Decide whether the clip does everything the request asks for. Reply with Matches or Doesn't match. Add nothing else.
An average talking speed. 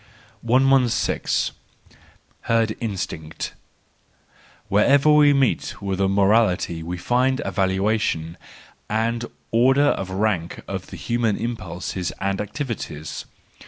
Doesn't match